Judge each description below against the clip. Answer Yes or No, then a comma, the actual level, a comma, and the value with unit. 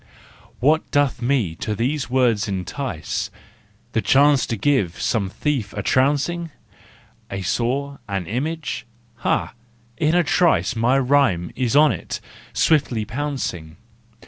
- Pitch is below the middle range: Yes, low, 130 Hz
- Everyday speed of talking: No, slow, 125 wpm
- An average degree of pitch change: No, wide, 5.7 semitones